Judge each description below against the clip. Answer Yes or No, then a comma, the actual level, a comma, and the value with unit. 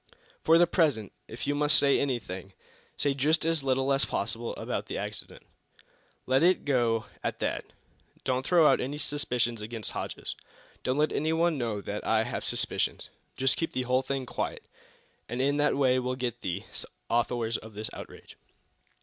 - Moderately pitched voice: No, low, 130 Hz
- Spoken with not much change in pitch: No, average, 3.9 semitones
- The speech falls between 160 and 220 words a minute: Yes, average, 175 wpm